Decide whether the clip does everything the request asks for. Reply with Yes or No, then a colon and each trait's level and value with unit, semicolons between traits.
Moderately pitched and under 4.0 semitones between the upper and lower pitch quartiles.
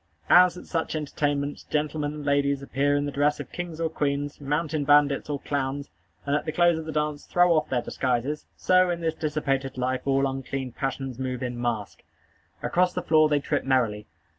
Yes: medium, 145 Hz; narrow, 2.5 semitones